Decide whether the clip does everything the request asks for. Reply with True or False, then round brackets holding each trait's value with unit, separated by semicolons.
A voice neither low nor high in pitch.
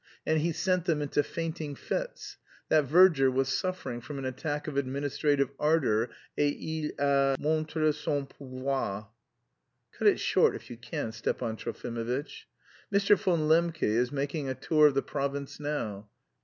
True (145 Hz)